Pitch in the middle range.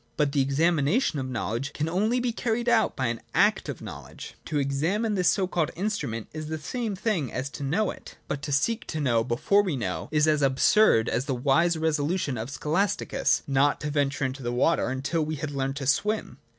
Yes: medium, 150 Hz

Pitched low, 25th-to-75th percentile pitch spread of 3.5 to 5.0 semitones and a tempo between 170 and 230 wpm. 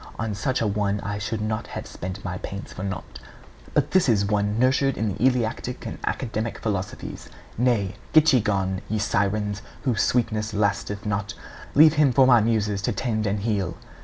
No: low, 105 Hz; average, 3.1 semitones; average, 185 wpm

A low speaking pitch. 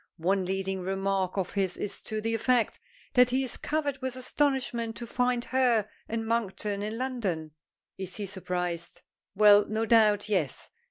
No: high, 215 Hz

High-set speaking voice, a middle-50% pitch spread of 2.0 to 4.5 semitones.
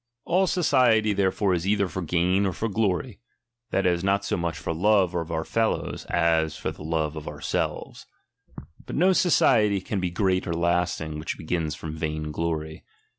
No: very low, 90 Hz; average, 3.9 semitones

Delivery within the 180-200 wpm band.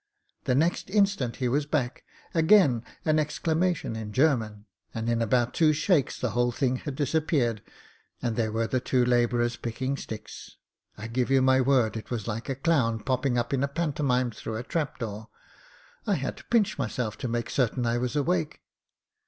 Yes: average, 185 wpm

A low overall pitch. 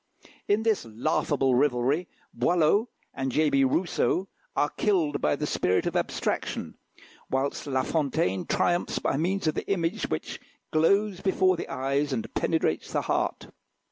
No: medium, 155 Hz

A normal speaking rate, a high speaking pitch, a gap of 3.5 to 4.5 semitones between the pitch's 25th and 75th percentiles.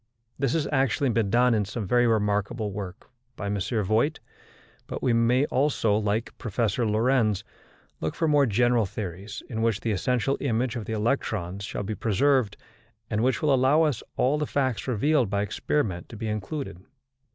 No: average, 170 wpm; low, 115 Hz; average, 4.1 semitones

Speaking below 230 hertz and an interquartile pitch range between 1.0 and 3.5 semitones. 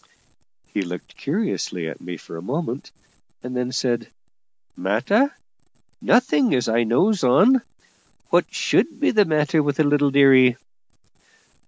No: low, 135 Hz; average, 5.2 semitones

